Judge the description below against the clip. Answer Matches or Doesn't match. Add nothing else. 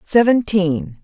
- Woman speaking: Matches